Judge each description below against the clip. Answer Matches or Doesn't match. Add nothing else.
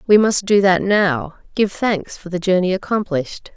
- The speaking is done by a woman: Matches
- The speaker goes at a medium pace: Matches